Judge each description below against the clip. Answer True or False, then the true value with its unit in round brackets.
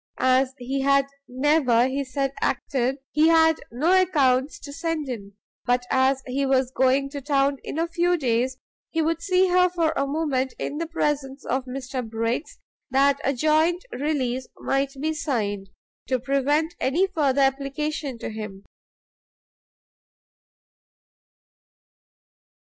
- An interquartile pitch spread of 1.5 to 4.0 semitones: True (3.2 semitones)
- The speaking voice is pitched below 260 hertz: False (275 Hz)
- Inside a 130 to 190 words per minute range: True (140 wpm)